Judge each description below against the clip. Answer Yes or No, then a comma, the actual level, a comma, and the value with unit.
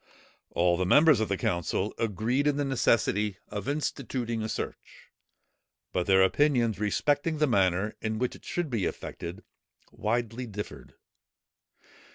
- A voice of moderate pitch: No, low, 110 Hz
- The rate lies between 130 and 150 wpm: Yes, average, 140 wpm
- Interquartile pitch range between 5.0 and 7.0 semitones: Yes, wide, 5.6 semitones